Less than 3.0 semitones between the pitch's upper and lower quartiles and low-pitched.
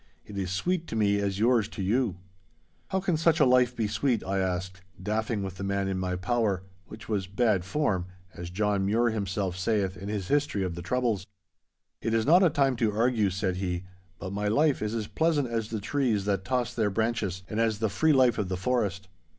No: average, 4.0 semitones; low, 105 Hz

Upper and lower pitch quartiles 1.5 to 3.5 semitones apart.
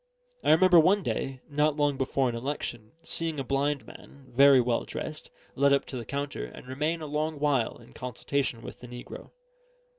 Yes: average, 3.0 semitones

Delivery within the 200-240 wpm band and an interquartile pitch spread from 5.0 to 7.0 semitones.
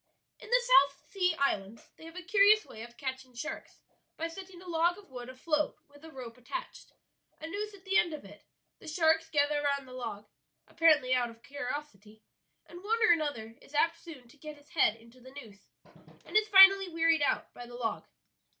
Yes: fast, 205 wpm; wide, 5.4 semitones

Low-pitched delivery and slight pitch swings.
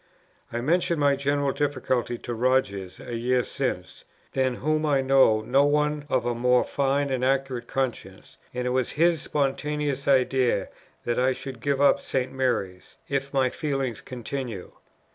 Yes: low, 130 Hz; narrow, 2.3 semitones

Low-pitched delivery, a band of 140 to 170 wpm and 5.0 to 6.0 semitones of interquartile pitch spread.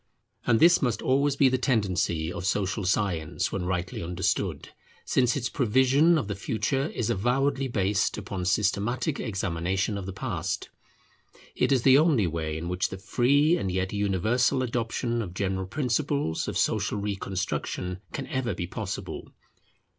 Yes: low, 105 Hz; average, 155 wpm; wide, 5.6 semitones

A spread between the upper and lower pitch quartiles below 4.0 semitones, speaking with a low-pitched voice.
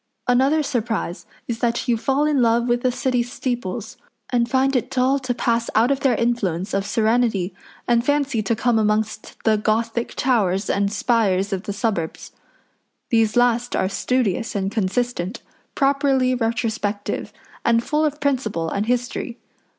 No: average, 3.0 semitones; high, 235 Hz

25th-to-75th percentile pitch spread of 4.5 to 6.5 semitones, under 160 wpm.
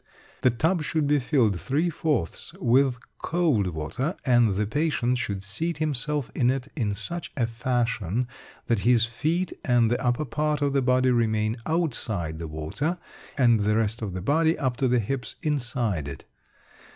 No: average, 5.2 semitones; average, 170 wpm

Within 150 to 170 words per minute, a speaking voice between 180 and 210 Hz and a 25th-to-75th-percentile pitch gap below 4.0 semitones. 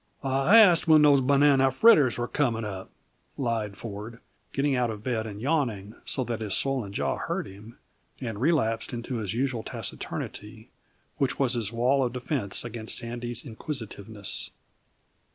No: average, 155 wpm; low, 120 Hz; average, 3.6 semitones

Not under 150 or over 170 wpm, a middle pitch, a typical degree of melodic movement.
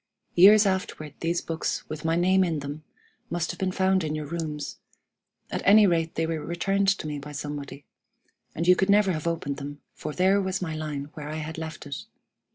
No: fast, 205 wpm; medium, 165 Hz; average, 3.7 semitones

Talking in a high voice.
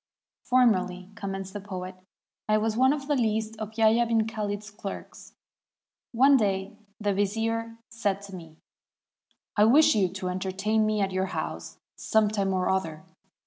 Yes: high, 210 Hz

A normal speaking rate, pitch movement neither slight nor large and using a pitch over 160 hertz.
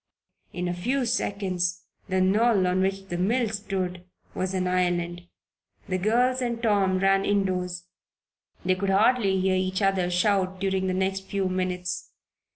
No: average, 155 wpm; narrow, 1.5 semitones; high, 190 Hz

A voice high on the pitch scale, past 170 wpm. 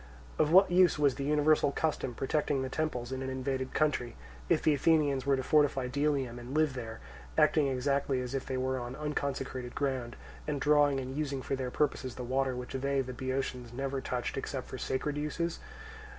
No: low, 135 Hz; average, 195 wpm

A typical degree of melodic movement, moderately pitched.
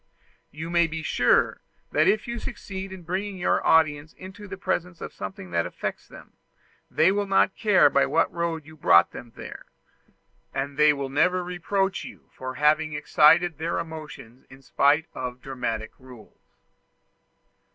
Yes: average, 4.8 semitones; medium, 160 Hz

